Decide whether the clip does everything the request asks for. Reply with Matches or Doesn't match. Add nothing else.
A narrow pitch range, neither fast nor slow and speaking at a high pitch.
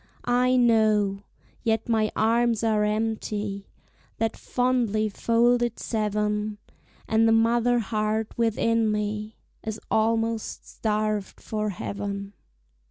Doesn't match